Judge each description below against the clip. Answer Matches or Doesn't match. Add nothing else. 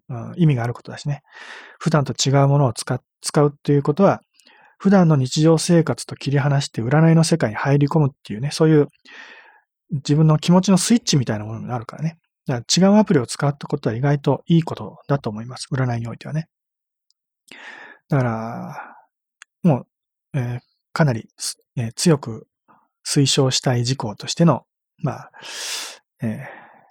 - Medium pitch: Matches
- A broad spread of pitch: Doesn't match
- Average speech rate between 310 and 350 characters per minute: Matches